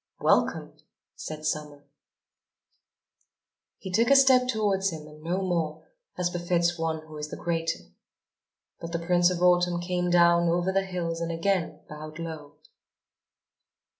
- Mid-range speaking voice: Yes, medium, 170 Hz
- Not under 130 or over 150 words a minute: Yes, average, 140 wpm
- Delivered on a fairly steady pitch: Yes, narrow, 2.1 semitones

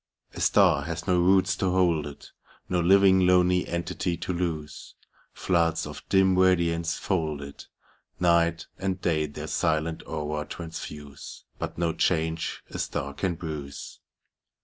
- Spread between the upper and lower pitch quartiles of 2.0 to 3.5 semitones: Yes, average, 2.7 semitones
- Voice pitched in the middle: No, very low, 85 Hz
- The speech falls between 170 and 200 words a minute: No, average, 140 wpm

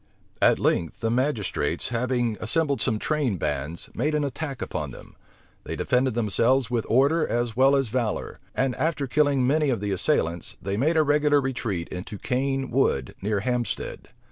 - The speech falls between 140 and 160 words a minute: No, average, 170 wpm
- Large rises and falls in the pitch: No, average, 4.6 semitones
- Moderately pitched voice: No, low, 125 Hz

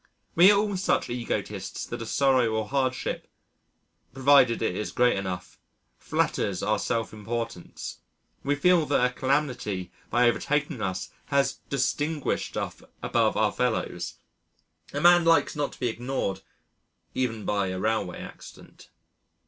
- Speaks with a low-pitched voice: Yes, low, 125 Hz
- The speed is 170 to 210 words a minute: No, average, 140 wpm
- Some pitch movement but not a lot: Yes, average, 4.7 semitones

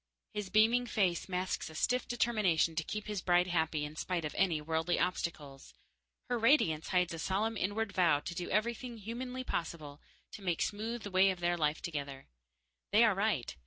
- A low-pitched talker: No, medium, 180 Hz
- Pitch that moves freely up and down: No, average, 5.0 semitones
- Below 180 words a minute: No, average, 185 wpm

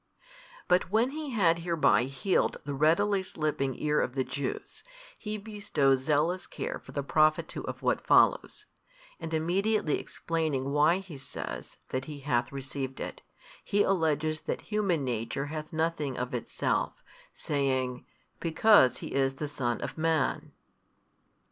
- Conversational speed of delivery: Yes, average, 145 wpm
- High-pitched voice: No, medium, 155 Hz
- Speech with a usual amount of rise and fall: Yes, average, 4.8 semitones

